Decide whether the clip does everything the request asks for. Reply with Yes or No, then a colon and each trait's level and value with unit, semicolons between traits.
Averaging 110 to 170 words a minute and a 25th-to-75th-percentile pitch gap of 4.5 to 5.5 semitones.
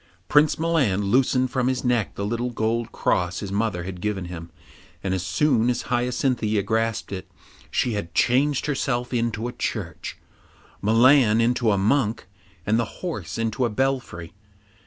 No: average, 155 wpm; average, 3.8 semitones